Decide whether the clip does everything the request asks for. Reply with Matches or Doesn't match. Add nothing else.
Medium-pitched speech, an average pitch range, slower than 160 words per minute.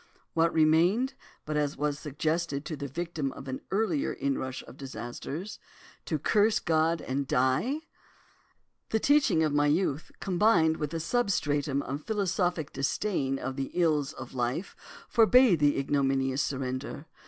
Matches